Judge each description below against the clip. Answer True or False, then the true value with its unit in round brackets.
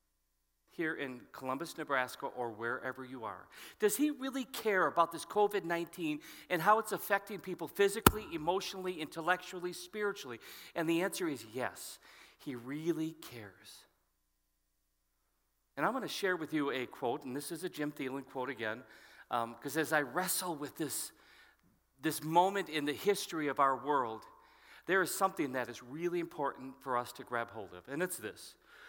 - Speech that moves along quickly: False (165 wpm)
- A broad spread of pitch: True (5.7 semitones)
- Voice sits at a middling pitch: True (160 Hz)